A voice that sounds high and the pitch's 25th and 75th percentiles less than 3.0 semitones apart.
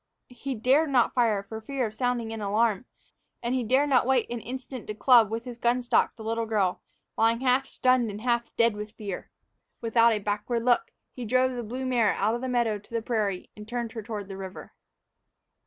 Yes: high, 230 Hz; narrow, 2.6 semitones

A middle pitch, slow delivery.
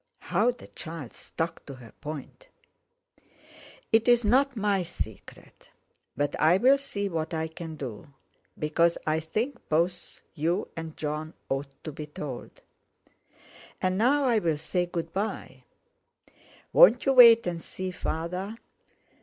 Yes: medium, 170 Hz; slow, 130 wpm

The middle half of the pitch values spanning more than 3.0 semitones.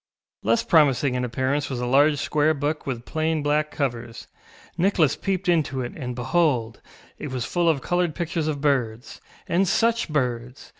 Yes: average, 4.1 semitones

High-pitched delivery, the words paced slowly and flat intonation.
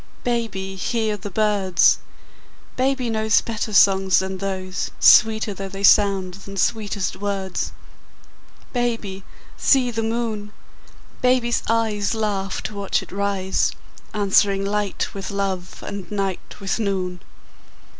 Yes: high, 200 Hz; slow, 120 wpm; narrow, 2.3 semitones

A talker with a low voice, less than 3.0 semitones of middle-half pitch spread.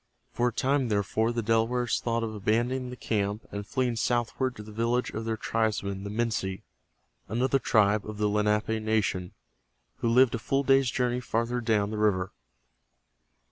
Yes: low, 115 Hz; narrow, 2.5 semitones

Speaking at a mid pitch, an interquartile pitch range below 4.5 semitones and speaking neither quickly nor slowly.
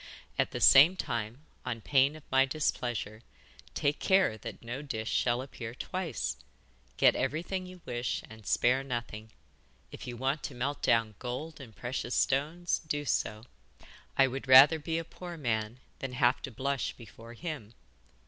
No: low, 130 Hz; average, 3.8 semitones; average, 160 wpm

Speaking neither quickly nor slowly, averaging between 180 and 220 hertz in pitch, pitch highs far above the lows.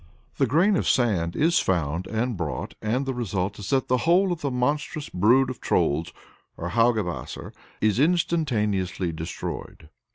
No: average, 155 wpm; low, 115 Hz; wide, 7.2 semitones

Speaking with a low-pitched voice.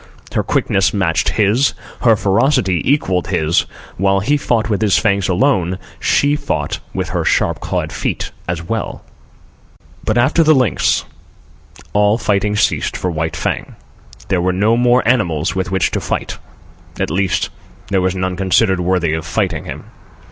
Yes: very low, 95 Hz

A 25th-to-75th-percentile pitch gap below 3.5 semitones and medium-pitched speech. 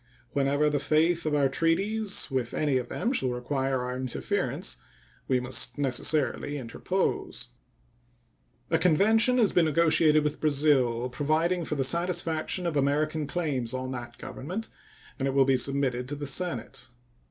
No: average, 4.0 semitones; medium, 145 Hz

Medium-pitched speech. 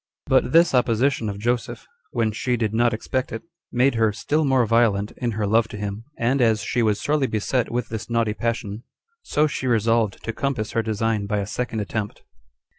No: low, 115 Hz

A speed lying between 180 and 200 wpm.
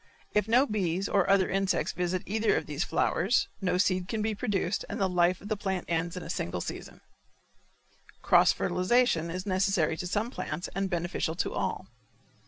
Yes: average, 185 wpm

